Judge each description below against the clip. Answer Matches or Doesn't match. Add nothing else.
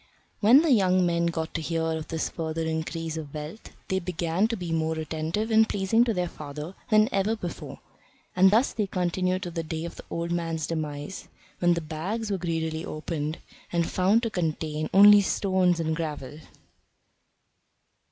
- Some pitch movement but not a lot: Matches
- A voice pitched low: Doesn't match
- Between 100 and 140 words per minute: Doesn't match